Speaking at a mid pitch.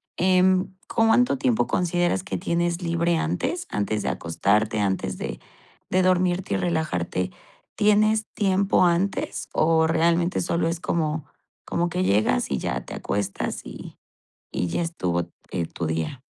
Yes: medium, 170 Hz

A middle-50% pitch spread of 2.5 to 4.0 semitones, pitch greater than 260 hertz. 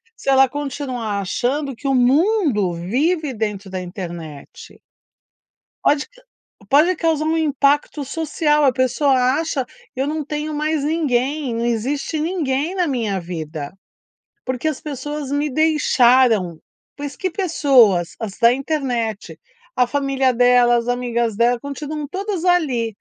No: average, 4.4 semitones; very high, 270 Hz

